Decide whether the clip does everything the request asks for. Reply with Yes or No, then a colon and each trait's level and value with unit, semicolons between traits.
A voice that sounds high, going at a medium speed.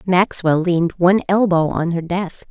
No: medium, 175 Hz; average, 170 wpm